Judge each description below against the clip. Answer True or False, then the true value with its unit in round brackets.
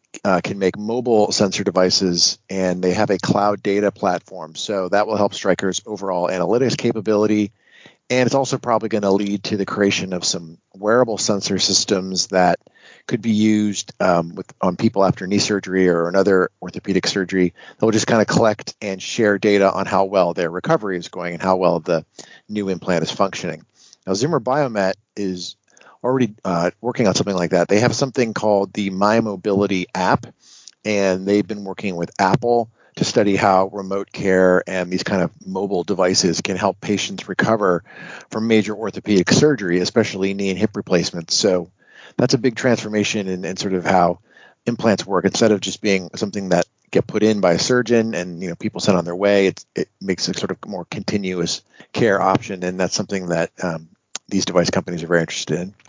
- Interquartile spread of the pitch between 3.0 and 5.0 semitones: False (2.5 semitones)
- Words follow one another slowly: False (190 wpm)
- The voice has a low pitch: True (100 Hz)